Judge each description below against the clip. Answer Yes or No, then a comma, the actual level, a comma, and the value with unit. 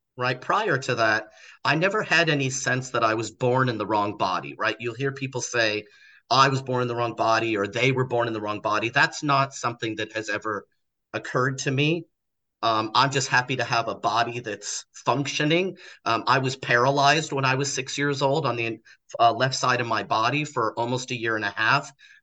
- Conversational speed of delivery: No, fast, 220 wpm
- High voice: No, low, 125 Hz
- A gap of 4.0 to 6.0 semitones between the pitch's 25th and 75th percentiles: No, average, 3.2 semitones